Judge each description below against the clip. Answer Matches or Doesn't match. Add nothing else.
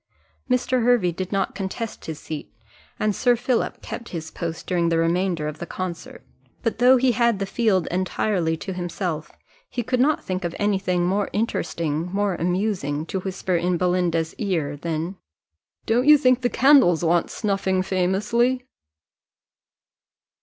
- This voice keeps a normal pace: Matches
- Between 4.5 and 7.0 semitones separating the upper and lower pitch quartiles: Matches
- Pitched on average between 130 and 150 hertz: Doesn't match